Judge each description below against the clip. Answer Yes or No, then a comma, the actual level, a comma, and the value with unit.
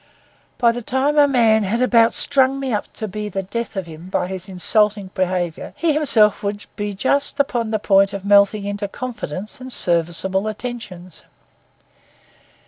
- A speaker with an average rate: Yes, average, 165 wpm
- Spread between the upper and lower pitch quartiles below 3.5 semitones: No, average, 4.1 semitones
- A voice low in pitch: No, high, 210 Hz